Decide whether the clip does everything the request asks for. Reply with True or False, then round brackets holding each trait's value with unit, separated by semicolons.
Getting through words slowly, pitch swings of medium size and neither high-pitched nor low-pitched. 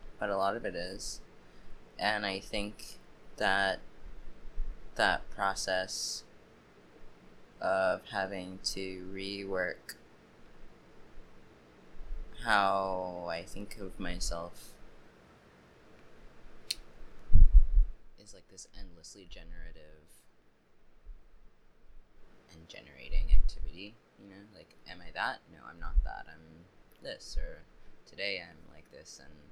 False (95 wpm; 4.5 semitones; 90 Hz)